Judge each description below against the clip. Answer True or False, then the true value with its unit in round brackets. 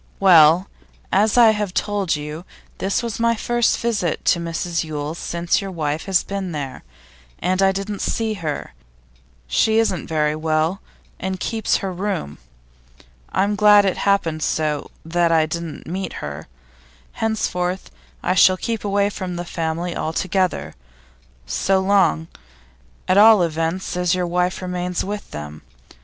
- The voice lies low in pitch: False (180 Hz)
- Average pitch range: True (3.6 semitones)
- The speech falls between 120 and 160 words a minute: True (145 wpm)